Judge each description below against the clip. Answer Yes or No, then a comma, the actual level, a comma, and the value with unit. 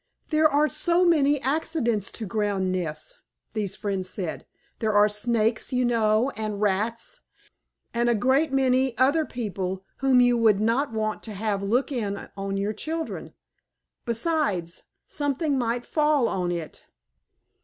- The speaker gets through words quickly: No, average, 145 wpm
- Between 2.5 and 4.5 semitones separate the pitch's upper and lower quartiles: No, average, 5.0 semitones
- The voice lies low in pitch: No, high, 230 Hz